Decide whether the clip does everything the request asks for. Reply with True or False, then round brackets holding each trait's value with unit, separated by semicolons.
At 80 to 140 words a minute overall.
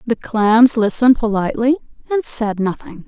True (135 wpm)